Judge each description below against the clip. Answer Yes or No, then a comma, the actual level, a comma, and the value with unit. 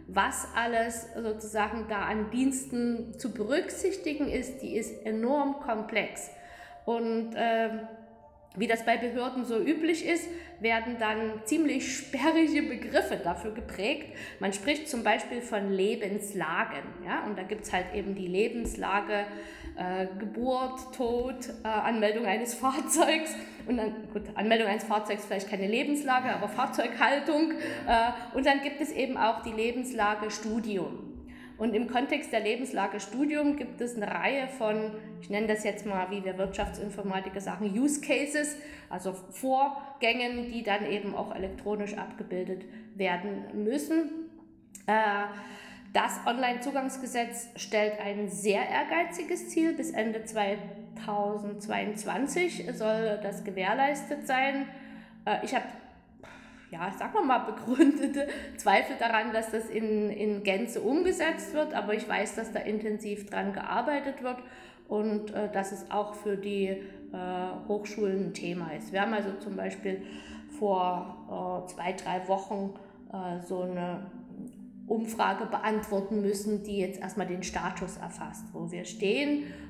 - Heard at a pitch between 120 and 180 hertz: No, high, 220 Hz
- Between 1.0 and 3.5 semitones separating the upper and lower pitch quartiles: No, average, 3.9 semitones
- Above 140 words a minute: No, average, 135 wpm